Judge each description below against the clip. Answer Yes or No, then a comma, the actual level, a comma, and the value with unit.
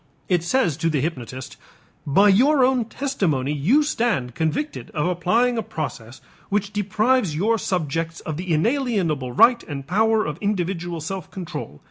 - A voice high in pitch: No, medium, 180 Hz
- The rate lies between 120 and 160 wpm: Yes, average, 150 wpm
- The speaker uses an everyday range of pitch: No, wide, 6.6 semitones